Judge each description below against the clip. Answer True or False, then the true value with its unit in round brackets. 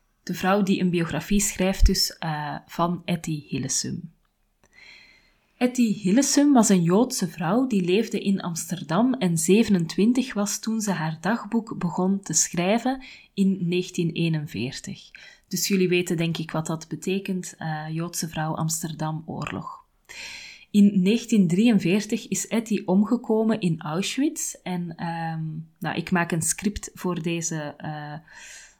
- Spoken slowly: True (130 wpm)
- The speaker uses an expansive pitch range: False (3.6 semitones)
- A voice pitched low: False (185 Hz)